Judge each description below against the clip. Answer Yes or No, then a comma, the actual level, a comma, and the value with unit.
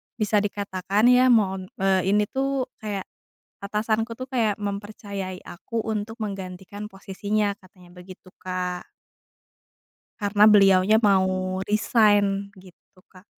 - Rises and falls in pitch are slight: Yes, narrow, 2.3 semitones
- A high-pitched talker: Yes, high, 200 Hz